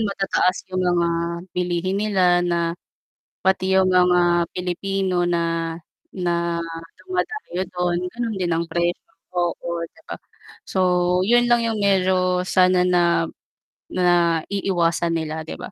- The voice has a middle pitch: Yes, medium, 180 Hz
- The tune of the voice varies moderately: No, narrow, 1.7 semitones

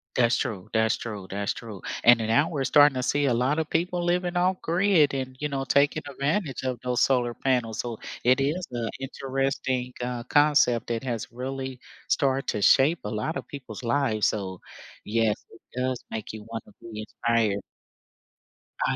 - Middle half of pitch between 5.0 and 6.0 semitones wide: No, average, 3.8 semitones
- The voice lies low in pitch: Yes, low, 130 Hz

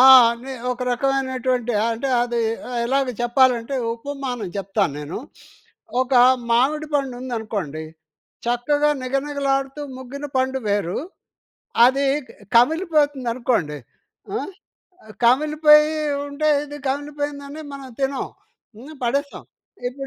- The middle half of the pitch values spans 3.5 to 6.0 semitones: No, average, 3.0 semitones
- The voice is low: No, very high, 265 Hz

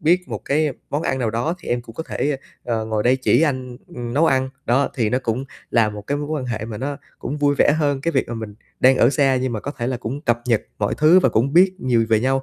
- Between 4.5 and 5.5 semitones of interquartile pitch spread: No, average, 3.6 semitones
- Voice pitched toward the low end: Yes, low, 130 Hz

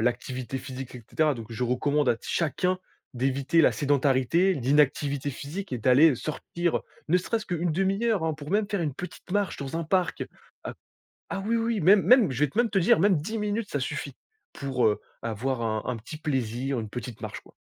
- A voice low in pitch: No, medium, 150 Hz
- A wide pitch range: Yes, wide, 6.1 semitones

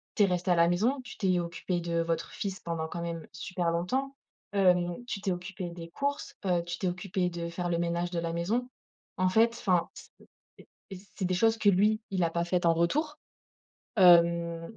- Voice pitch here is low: No, medium, 180 Hz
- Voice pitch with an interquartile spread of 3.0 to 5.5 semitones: No, narrow, 2.6 semitones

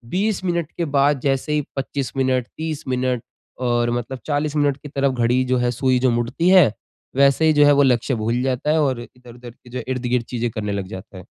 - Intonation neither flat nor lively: Yes, average, 3.1 semitones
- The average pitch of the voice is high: No, low, 130 Hz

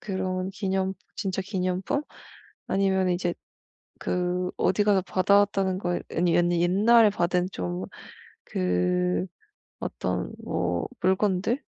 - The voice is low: No, medium, 185 Hz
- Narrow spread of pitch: Yes, narrow, 1.9 semitones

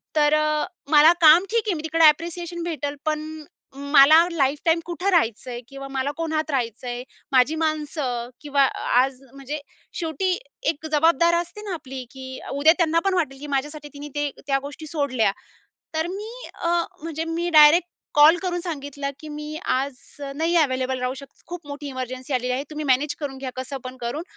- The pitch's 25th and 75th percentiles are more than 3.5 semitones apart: No, average, 3.2 semitones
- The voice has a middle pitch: No, very high, 295 Hz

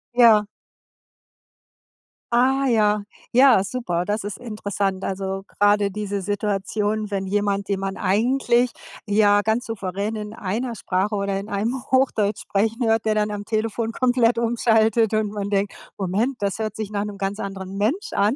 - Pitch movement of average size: No, narrow, 2.3 semitones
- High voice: Yes, high, 210 Hz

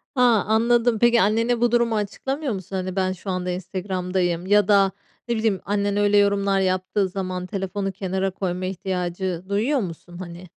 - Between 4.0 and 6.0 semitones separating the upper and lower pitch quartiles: No, narrow, 2.6 semitones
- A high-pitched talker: Yes, high, 195 Hz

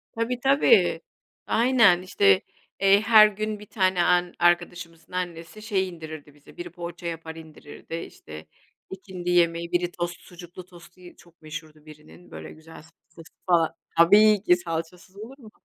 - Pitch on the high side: No, medium, 175 Hz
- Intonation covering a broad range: No, average, 2.8 semitones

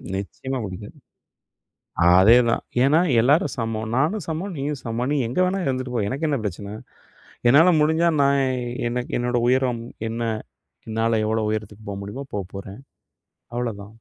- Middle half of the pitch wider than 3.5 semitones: Yes, average, 4.4 semitones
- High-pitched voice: No, low, 120 Hz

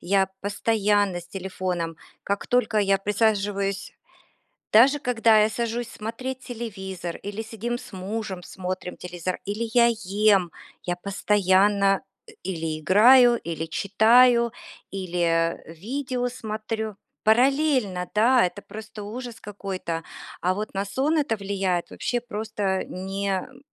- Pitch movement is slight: No, average, 3.5 semitones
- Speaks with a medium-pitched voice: No, high, 205 Hz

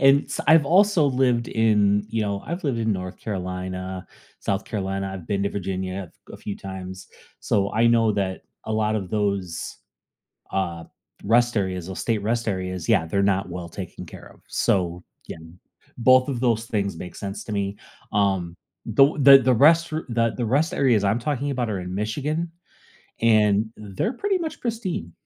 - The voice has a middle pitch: No, low, 105 Hz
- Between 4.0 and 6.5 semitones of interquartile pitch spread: Yes, average, 4.4 semitones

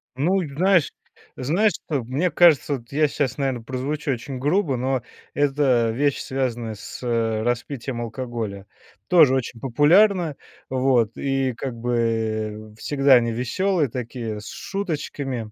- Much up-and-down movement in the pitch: No, average, 3.9 semitones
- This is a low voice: Yes, low, 130 Hz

